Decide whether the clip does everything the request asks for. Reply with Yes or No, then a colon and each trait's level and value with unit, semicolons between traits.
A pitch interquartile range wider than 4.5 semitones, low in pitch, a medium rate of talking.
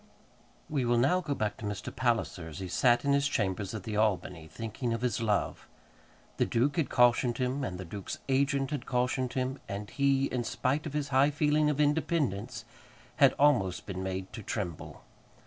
Yes: average, 5.2 semitones; low, 120 Hz; average, 190 wpm